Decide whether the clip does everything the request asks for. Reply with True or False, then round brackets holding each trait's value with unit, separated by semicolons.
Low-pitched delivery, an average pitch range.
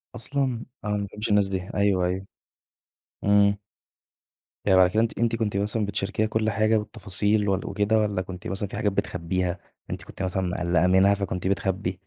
False (100 Hz; 2.2 semitones)